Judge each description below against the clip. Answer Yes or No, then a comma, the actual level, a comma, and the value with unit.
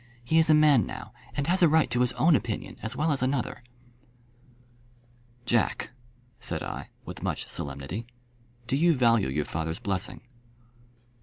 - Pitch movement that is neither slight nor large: No, wide, 6.9 semitones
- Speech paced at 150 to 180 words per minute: Yes, average, 155 wpm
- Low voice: Yes, low, 125 Hz